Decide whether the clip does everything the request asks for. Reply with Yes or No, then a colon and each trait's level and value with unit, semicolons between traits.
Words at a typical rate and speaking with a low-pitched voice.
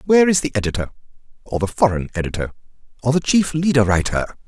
Yes: average, 175 wpm; low, 125 Hz